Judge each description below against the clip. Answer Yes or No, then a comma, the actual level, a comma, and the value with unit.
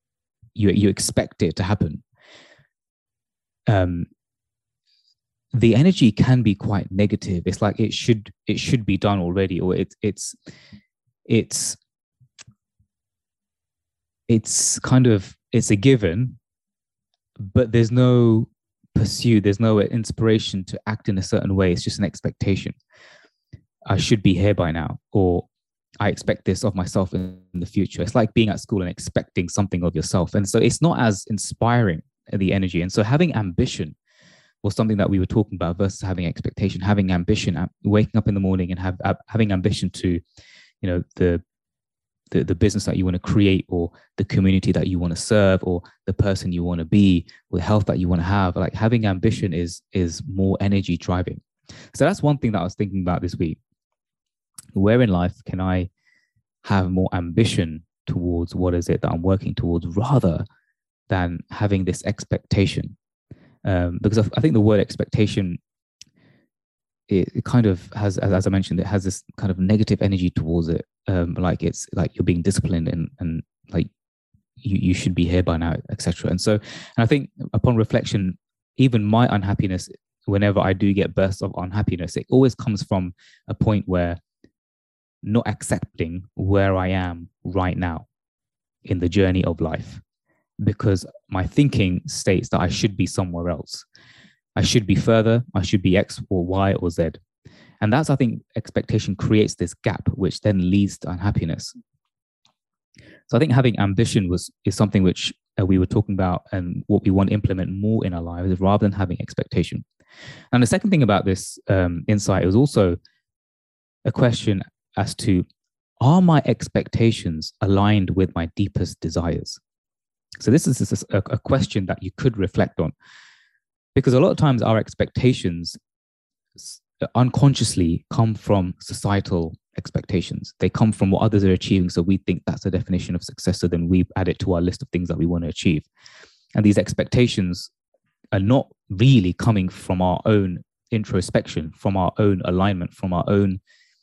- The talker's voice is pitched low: Yes, low, 100 Hz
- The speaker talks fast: No, average, 170 wpm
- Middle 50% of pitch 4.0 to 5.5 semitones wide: No, average, 3.5 semitones